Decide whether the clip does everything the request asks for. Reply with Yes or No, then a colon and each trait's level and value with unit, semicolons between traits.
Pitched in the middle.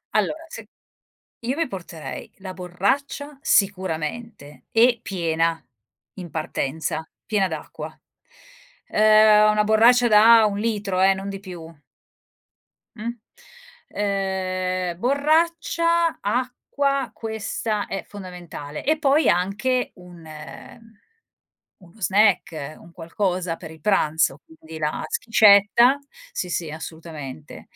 No: high, 195 Hz